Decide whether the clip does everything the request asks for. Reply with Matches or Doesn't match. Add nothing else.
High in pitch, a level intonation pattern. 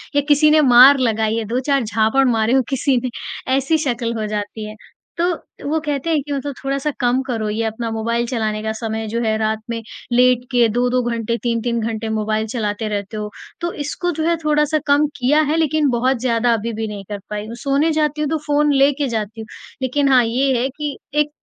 Doesn't match